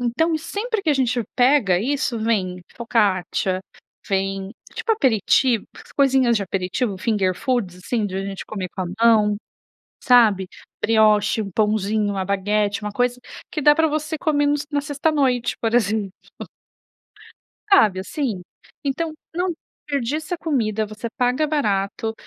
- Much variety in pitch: Yes, wide, 6.0 semitones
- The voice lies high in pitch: Yes, high, 230 Hz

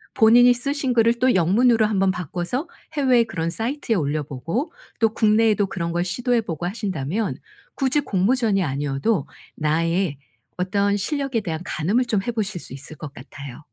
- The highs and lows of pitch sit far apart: Yes, wide, 6.1 semitones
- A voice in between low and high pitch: No, high, 200 Hz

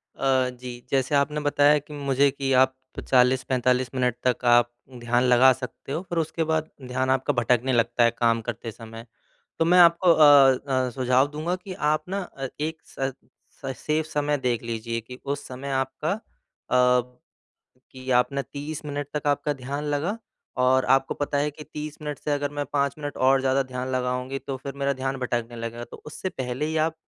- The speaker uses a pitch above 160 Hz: No, low, 135 Hz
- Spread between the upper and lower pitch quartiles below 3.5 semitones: Yes, average, 2.8 semitones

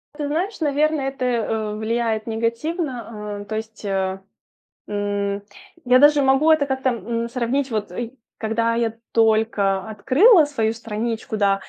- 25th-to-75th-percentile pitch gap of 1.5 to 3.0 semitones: No, average, 4.0 semitones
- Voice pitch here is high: Yes, high, 230 Hz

